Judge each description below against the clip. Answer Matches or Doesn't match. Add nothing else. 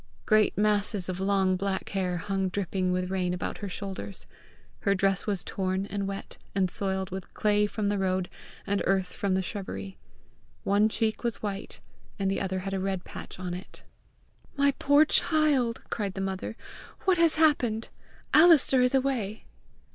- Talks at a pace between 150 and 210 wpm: Matches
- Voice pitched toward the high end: Matches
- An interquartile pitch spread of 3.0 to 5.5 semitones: Doesn't match